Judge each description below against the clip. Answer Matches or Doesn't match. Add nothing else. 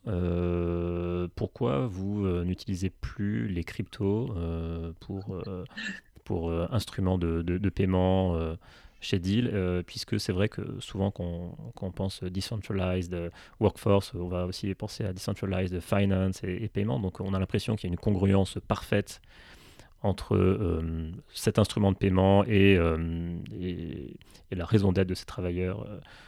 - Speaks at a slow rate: Doesn't match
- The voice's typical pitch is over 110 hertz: Doesn't match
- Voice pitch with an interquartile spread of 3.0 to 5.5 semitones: Doesn't match